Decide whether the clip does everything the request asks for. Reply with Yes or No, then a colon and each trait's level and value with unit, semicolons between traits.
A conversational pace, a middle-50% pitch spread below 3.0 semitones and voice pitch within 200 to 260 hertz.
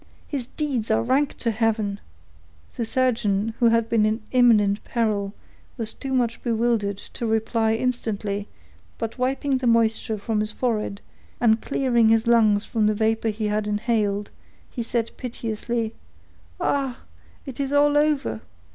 Yes: average, 145 wpm; narrow, 2.4 semitones; high, 225 Hz